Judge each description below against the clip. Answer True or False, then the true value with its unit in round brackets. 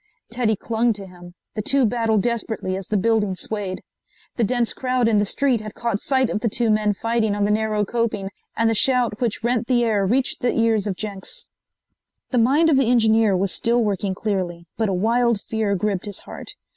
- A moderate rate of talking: False (210 wpm)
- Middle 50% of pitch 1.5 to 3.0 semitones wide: True (2.7 semitones)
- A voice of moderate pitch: False (220 Hz)